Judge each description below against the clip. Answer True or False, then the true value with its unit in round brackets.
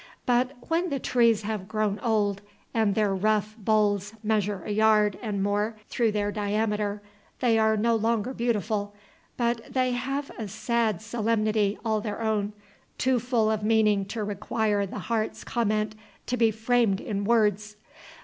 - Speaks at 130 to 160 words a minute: True (155 wpm)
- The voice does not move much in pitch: True (1.9 semitones)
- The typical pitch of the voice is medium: False (215 Hz)